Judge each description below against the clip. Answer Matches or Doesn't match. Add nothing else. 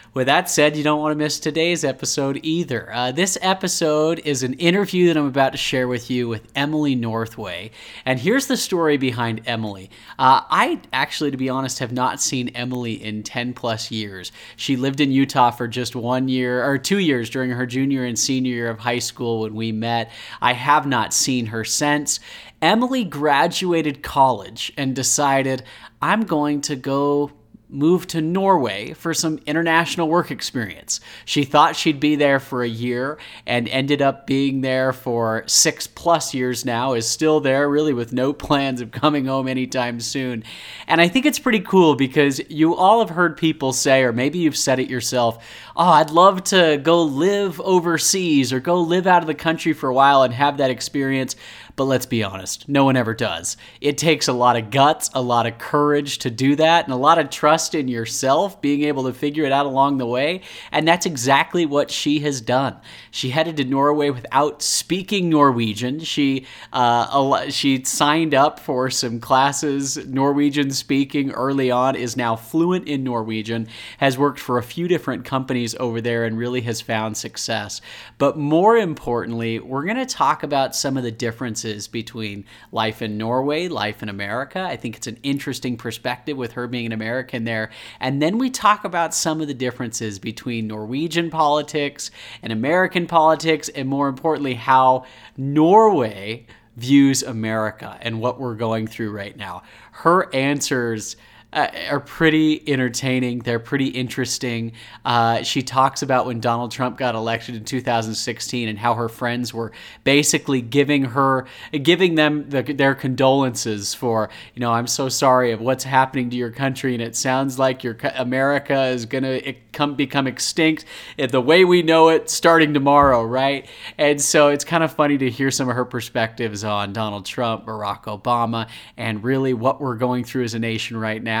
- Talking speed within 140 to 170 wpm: Doesn't match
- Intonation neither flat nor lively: Matches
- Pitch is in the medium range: Doesn't match